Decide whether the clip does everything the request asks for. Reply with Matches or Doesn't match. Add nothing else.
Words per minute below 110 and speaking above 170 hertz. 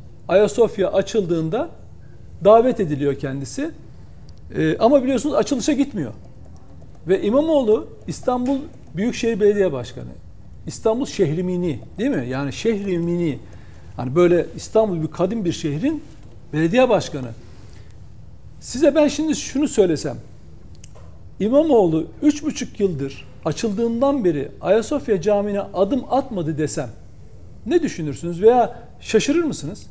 Matches